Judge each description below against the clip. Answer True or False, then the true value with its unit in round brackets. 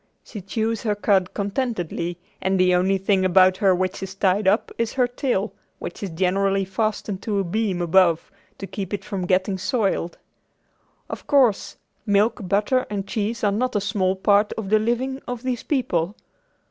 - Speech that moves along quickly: False (175 wpm)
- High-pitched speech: True (200 Hz)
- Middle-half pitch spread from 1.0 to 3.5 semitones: True (2.8 semitones)